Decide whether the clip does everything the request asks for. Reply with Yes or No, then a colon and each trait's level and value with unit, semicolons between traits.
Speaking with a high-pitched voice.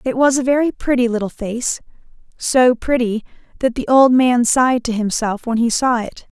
Yes: high, 245 Hz